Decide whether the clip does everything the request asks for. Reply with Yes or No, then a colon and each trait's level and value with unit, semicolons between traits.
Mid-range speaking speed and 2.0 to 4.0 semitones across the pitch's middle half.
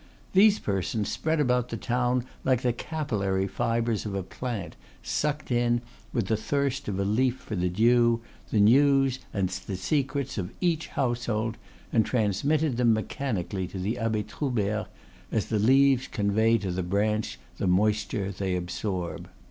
No: average, 155 wpm; average, 4.4 semitones